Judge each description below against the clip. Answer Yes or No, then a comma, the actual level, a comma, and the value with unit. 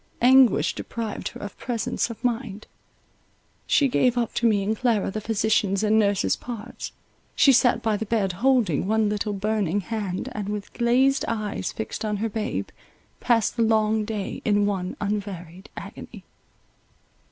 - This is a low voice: No, high, 215 Hz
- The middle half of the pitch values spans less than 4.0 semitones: Yes, narrow, 2.4 semitones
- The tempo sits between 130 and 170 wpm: Yes, average, 155 wpm